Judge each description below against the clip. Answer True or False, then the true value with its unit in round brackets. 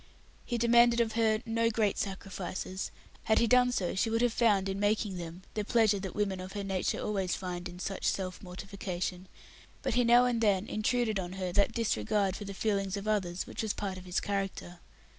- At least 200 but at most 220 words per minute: True (205 wpm)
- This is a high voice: True (200 Hz)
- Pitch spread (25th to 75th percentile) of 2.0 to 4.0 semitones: True (3.1 semitones)